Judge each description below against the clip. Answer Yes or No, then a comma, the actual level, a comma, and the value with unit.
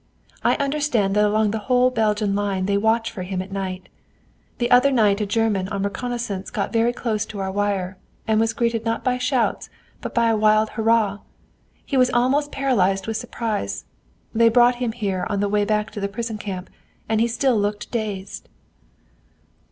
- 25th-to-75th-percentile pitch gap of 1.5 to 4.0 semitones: Yes, average, 2.9 semitones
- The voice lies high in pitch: Yes, high, 215 Hz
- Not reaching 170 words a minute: No, average, 185 wpm